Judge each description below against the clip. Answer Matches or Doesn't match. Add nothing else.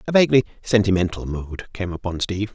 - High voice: Doesn't match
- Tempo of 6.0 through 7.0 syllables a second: Matches